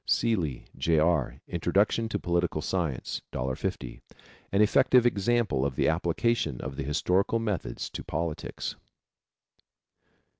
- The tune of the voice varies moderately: No, wide, 6.3 semitones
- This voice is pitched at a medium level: No, very low, 85 Hz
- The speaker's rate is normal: No, slow, 115 wpm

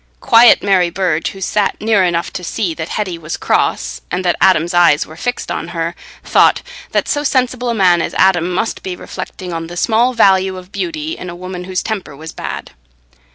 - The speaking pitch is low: No, medium, 185 Hz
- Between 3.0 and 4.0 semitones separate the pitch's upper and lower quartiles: Yes, average, 3.6 semitones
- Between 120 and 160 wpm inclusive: No, average, 200 wpm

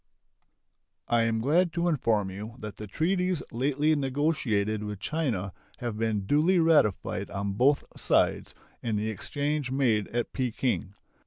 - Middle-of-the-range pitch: No, low, 120 Hz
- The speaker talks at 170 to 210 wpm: No, average, 140 wpm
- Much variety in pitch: Yes, wide, 5.9 semitones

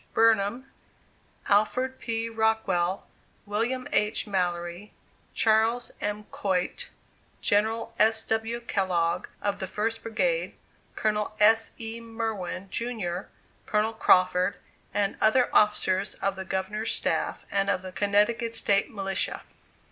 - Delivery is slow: Yes, slow, 115 wpm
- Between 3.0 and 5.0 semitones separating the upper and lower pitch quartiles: No, narrow, 2.6 semitones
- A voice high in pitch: Yes, high, 210 Hz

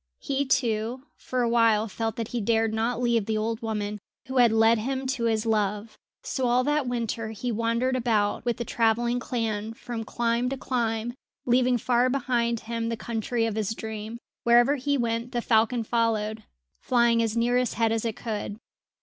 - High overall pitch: Yes, high, 230 Hz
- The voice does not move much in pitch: Yes, narrow, 1.7 semitones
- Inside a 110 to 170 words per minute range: No, average, 185 wpm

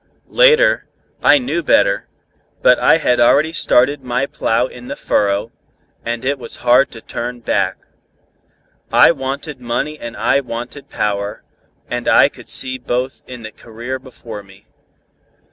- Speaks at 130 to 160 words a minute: Yes, average, 145 wpm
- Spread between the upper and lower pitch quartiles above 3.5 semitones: No, average, 3.2 semitones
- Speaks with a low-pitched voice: Yes, low, 125 Hz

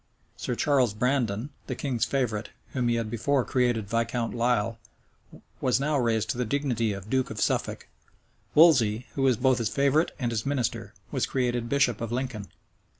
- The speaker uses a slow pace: No, average, 170 wpm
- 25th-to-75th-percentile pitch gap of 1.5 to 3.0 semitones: Yes, average, 2.7 semitones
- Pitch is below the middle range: Yes, low, 120 Hz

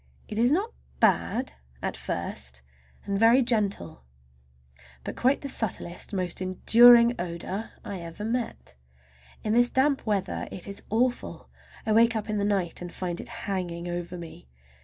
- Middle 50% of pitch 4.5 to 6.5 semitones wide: Yes, average, 5.1 semitones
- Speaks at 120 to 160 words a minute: Yes, average, 150 wpm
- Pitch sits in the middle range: No, high, 200 Hz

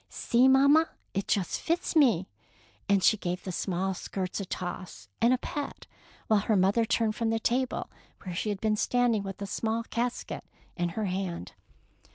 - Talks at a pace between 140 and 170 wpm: No, average, 185 wpm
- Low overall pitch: No, high, 215 Hz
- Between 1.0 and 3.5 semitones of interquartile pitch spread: No, average, 4.2 semitones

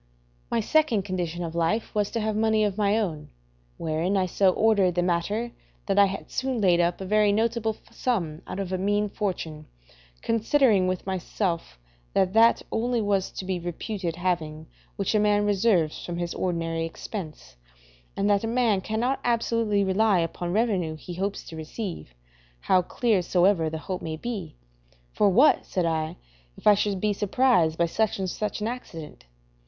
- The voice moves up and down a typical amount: Yes, average, 3.9 semitones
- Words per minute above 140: Yes, average, 175 wpm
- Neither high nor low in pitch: No, high, 195 Hz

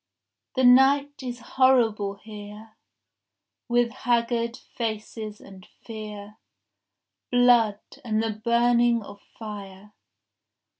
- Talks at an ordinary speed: No, slow, 95 wpm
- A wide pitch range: No, narrow, 2.5 semitones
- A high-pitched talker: Yes, high, 225 Hz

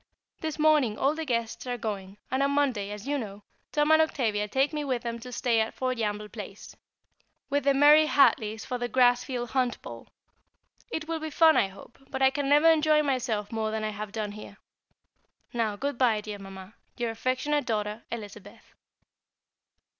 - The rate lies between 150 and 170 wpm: No, average, 185 wpm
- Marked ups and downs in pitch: No, average, 5.0 semitones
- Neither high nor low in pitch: No, high, 245 Hz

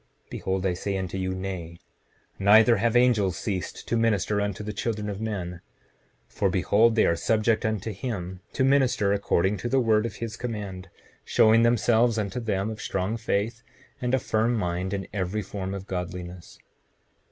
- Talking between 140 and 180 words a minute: Yes, average, 175 wpm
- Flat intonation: No, average, 3.3 semitones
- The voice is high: No, low, 105 Hz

